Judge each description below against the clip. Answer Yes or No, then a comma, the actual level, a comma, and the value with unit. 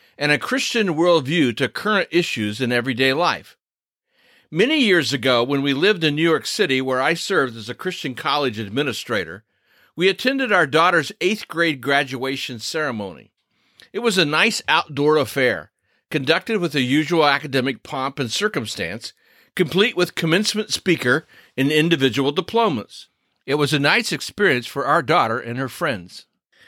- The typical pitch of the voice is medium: Yes, medium, 150 Hz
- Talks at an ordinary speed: Yes, average, 155 wpm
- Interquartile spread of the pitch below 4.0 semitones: No, average, 5.1 semitones